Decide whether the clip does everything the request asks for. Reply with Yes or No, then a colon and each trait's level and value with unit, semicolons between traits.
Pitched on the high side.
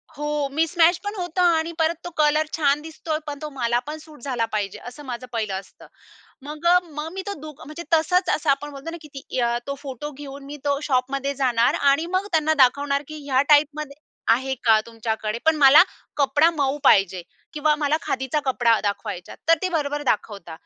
Yes: very high, 290 Hz